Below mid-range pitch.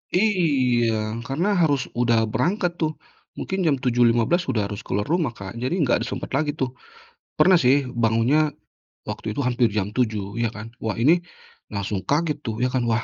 Yes: low, 125 Hz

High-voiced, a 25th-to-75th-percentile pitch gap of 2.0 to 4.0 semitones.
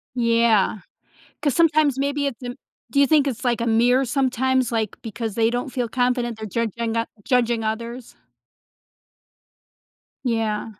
Yes: high, 240 Hz; narrow, 2.4 semitones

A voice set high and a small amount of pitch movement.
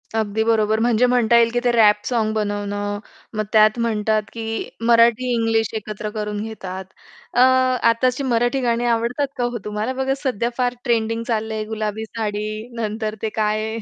Yes: high, 225 Hz; narrow, 1.7 semitones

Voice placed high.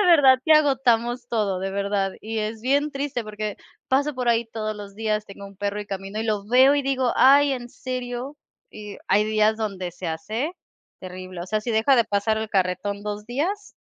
Yes: high, 220 Hz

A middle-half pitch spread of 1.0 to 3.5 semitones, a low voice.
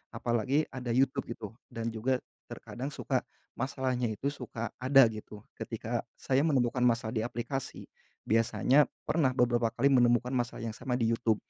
Yes: narrow, 2.4 semitones; low, 125 Hz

